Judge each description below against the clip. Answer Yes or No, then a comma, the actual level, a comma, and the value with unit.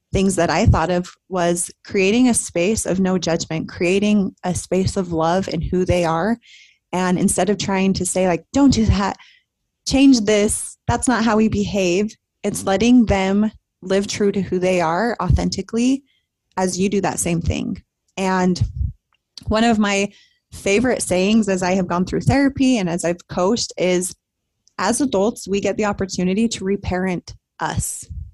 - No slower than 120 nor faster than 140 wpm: No, average, 170 wpm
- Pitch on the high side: Yes, high, 195 Hz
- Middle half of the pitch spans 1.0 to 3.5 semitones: Yes, average, 3.0 semitones